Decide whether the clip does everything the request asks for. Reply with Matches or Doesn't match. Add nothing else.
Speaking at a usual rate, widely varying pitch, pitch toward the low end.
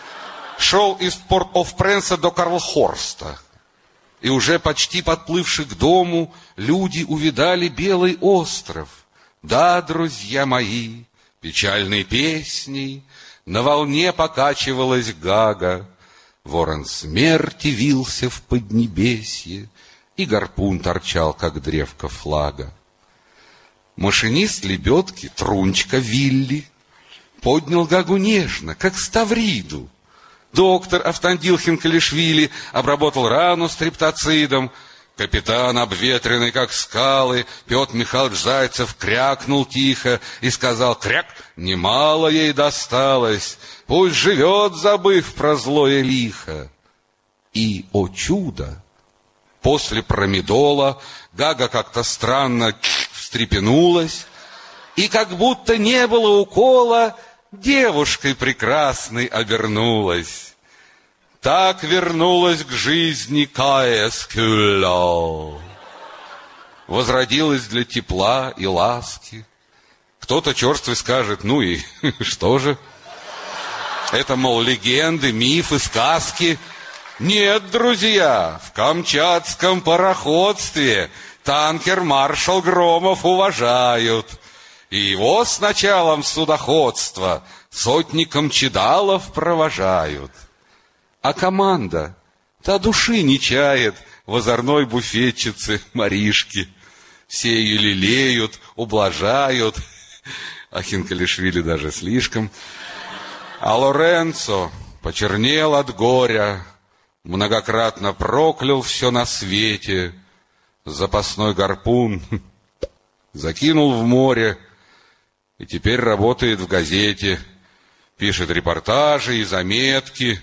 Doesn't match